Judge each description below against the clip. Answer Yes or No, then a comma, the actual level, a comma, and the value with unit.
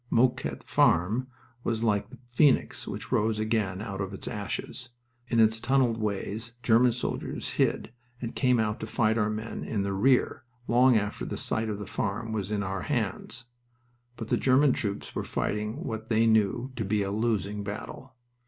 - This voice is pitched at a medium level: No, low, 110 Hz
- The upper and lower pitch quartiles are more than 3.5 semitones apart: No, narrow, 2.5 semitones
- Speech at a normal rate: Yes, average, 180 wpm